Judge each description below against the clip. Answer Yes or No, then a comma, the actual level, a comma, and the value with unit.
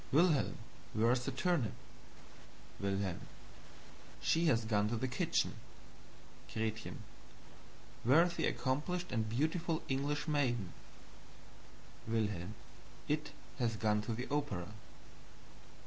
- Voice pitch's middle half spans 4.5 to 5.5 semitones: Yes, average, 5.2 semitones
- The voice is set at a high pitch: No, low, 120 Hz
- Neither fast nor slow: No, slow, 105 wpm